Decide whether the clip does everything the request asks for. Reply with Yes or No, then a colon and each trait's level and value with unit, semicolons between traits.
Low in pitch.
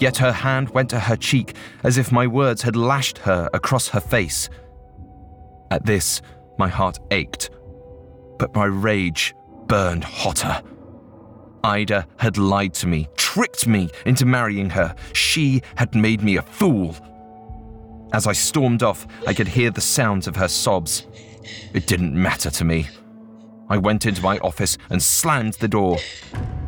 Yes: low, 110 Hz